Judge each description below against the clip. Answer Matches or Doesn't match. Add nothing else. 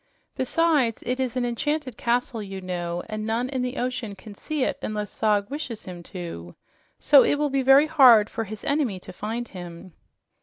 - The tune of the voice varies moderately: Matches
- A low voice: Doesn't match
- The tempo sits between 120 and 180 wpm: Doesn't match